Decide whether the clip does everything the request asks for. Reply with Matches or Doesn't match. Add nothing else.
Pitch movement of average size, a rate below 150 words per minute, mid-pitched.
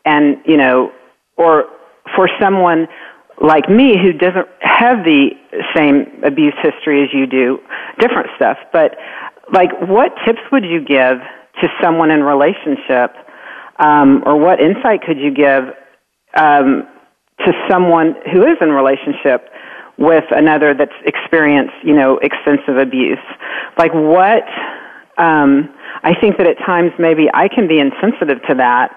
Matches